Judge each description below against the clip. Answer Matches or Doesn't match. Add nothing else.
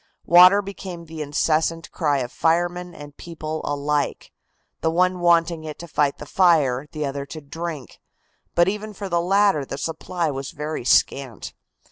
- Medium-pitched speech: Matches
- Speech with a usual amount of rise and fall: Matches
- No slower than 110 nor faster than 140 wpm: Doesn't match